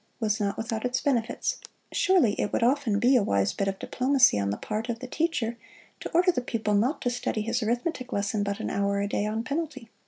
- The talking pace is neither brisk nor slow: No, fast, 225 wpm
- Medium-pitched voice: No, high, 230 Hz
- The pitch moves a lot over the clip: No, average, 3.6 semitones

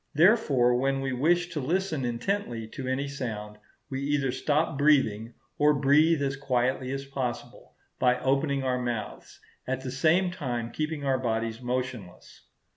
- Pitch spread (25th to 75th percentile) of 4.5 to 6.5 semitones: No, average, 3.0 semitones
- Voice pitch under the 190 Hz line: Yes, low, 135 Hz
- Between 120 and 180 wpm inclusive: Yes, average, 150 wpm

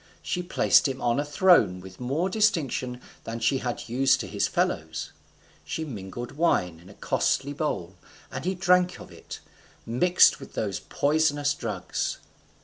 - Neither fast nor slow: Yes, average, 155 wpm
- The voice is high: No, low, 135 Hz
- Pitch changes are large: Yes, wide, 6.3 semitones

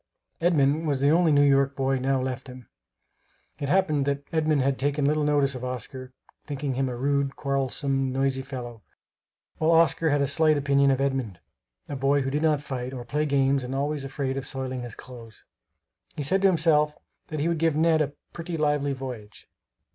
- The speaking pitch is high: No, medium, 140 Hz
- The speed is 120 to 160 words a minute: No, average, 190 wpm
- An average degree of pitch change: No, narrow, 2.2 semitones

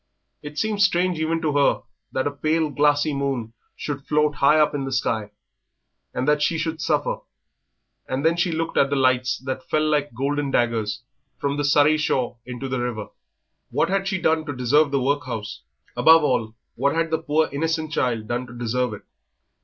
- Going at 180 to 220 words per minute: Yes, average, 190 wpm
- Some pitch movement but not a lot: Yes, average, 3.7 semitones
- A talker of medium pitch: Yes, medium, 145 Hz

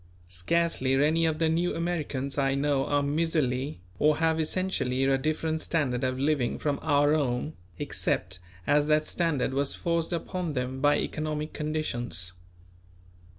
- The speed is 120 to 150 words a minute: Yes, average, 145 wpm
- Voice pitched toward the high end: No, medium, 145 Hz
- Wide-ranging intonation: No, average, 3.2 semitones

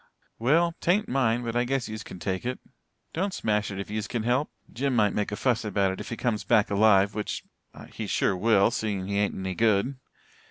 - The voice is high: No, low, 110 Hz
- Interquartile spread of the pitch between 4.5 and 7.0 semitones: No, average, 3.5 semitones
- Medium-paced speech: No, fast, 215 wpm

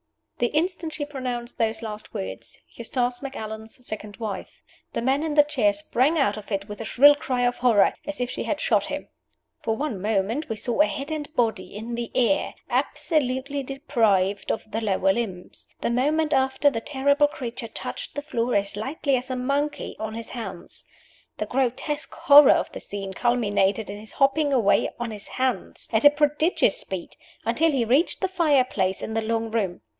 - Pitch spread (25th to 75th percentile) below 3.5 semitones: No, average, 4.8 semitones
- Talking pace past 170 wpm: Yes, average, 190 wpm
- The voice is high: Yes, high, 245 Hz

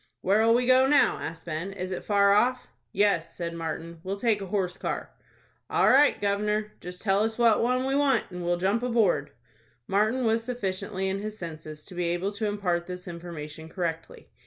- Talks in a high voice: Yes, high, 200 Hz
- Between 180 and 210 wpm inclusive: Yes, average, 190 wpm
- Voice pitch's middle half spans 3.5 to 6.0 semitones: Yes, average, 4.2 semitones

